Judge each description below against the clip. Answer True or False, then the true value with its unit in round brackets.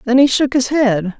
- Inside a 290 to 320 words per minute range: False (250 wpm)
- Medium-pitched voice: False (250 Hz)